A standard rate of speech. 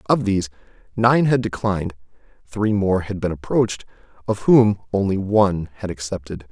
Yes: average, 145 wpm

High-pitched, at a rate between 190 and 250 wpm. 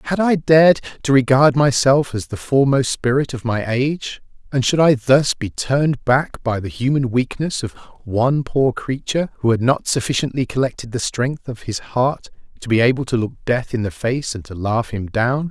No: low, 130 Hz; average, 200 wpm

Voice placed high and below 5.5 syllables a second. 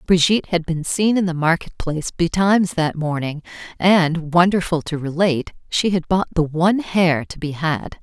No: medium, 170 Hz; 5.0 syllables/s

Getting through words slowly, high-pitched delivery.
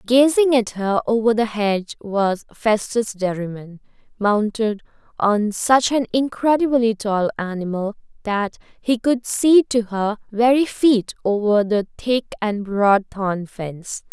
Yes: slow, 130 wpm; high, 220 Hz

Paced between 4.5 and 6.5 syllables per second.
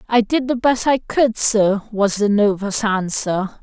No: 3.8 syllables/s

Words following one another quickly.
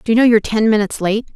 Yes: fast, 310 wpm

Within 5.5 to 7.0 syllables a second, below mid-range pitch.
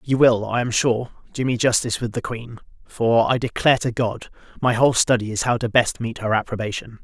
Yes: 5.7 syllables/s; low, 115 Hz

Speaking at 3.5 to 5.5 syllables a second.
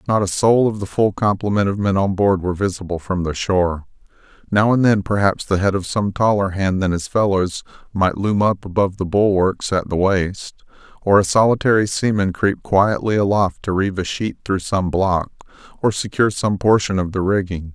Yes: 5.2 syllables/s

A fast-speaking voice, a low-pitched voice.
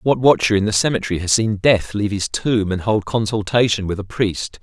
Yes: fast, 220 wpm; low, 105 Hz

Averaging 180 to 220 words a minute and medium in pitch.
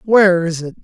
Yes: fast, 215 wpm; medium, 180 Hz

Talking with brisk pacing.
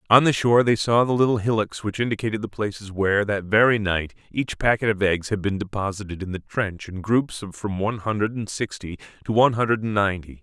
Yes: fast, 225 wpm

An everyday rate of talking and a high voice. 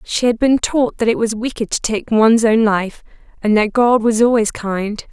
No: fast, 225 wpm; high, 225 Hz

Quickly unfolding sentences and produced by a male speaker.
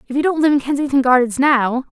No: fast, 245 wpm; female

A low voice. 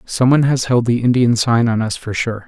Yes: low, 120 Hz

